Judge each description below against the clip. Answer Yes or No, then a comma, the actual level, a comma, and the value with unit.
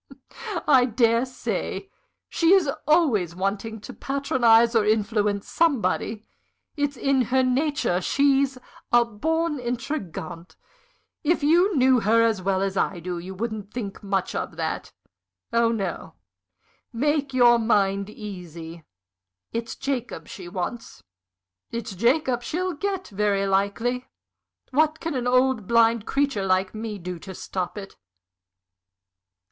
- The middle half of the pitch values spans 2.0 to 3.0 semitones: No, wide, 5.5 semitones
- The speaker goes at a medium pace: No, slow, 130 wpm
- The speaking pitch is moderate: No, high, 230 Hz